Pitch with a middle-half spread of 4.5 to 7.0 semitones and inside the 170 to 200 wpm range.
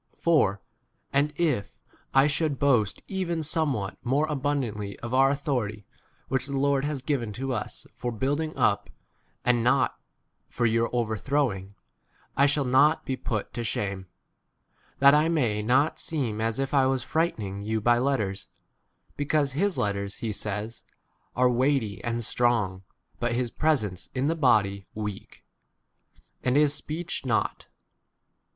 No: average, 4.8 semitones; average, 155 wpm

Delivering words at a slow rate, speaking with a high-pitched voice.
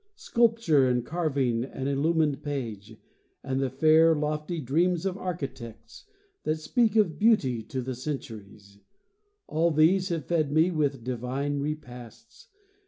No: slow, 130 wpm; medium, 145 Hz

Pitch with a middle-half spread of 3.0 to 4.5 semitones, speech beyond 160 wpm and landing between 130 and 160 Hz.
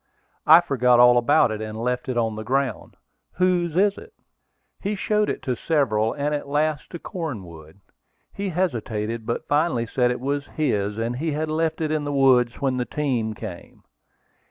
No: average, 5.3 semitones; average, 180 wpm; low, 135 Hz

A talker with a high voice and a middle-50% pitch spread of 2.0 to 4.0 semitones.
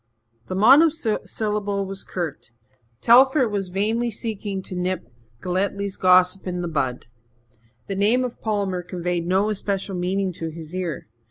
Yes: high, 195 Hz; average, 2.9 semitones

